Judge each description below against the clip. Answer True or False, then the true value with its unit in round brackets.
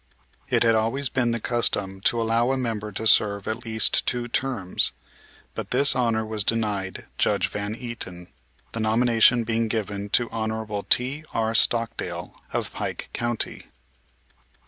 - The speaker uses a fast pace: False (145 wpm)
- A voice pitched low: True (115 Hz)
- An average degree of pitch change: False (2.0 semitones)